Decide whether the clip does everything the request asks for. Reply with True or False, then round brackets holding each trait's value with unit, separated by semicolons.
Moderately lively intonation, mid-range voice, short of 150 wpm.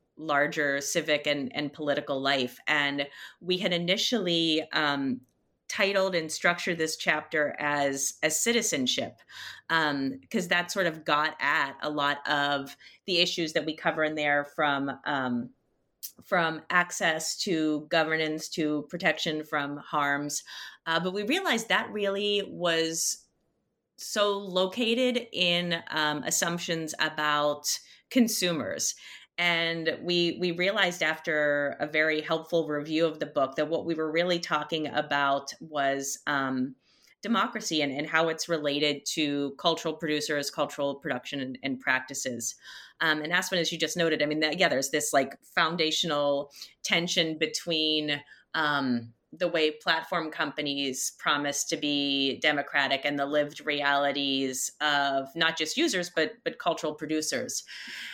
True (3.0 semitones; 155 Hz; 135 wpm)